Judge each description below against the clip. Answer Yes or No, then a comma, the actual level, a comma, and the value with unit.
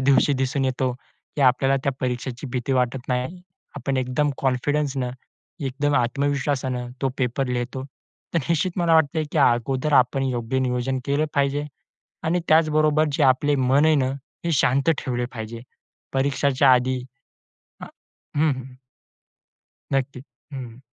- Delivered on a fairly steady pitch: Yes, narrow, 2.3 semitones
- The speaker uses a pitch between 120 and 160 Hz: Yes, low, 135 Hz